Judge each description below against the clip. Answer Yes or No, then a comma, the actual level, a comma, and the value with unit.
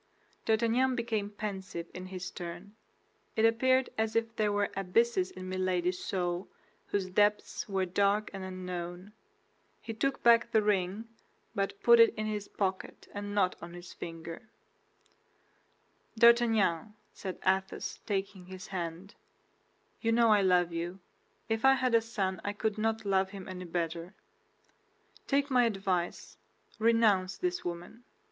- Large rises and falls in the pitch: No, average, 3.4 semitones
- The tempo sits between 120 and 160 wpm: Yes, average, 140 wpm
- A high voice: Yes, high, 200 Hz